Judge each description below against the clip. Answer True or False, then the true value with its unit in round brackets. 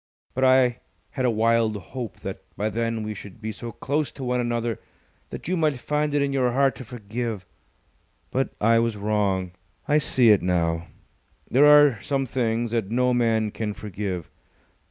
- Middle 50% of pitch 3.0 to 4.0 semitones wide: True (3.5 semitones)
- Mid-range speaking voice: False (115 Hz)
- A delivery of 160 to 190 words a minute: True (175 wpm)